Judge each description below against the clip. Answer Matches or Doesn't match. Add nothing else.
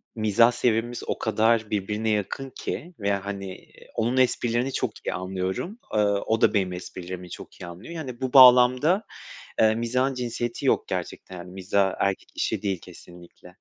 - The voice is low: Matches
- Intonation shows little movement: Doesn't match